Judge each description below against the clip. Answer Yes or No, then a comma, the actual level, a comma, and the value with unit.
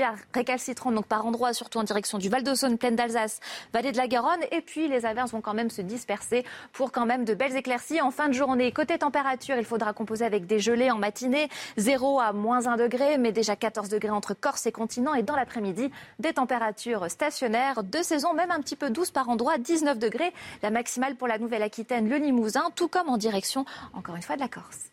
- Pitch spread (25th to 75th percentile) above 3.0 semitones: Yes, average, 3.4 semitones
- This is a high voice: Yes, high, 245 Hz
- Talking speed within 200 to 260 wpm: Yes, fast, 220 wpm